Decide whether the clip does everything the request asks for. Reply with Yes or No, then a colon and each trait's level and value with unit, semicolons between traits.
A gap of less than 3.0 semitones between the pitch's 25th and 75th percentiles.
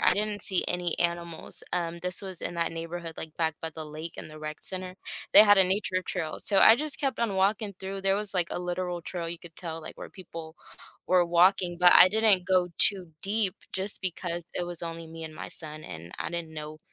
Yes: narrow, 2.6 semitones